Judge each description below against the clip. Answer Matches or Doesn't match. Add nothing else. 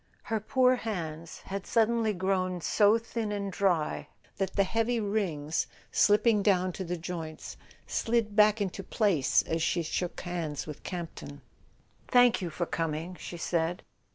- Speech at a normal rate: Matches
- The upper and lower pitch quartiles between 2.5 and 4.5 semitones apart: Matches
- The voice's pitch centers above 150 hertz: Matches